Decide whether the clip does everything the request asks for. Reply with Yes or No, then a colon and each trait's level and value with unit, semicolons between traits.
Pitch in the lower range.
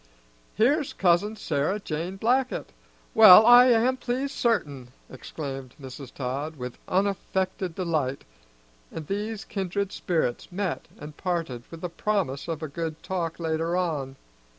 No: medium, 175 Hz